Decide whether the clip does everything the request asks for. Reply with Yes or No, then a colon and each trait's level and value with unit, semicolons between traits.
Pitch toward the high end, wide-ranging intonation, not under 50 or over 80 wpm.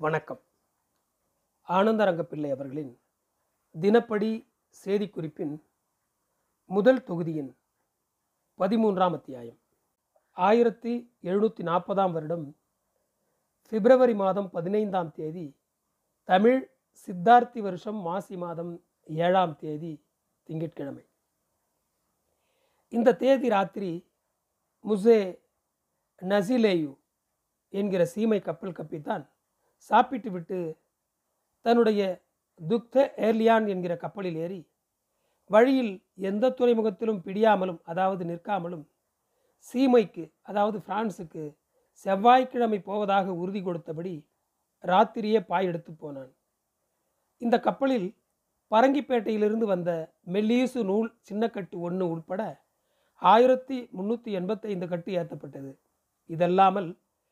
No: high, 195 Hz; average, 4.8 semitones; slow, 75 wpm